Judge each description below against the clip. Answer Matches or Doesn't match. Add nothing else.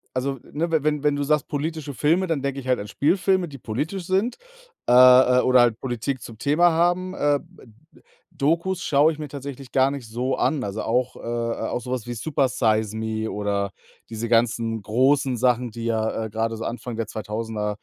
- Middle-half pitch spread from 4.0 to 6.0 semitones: Matches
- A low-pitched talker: Matches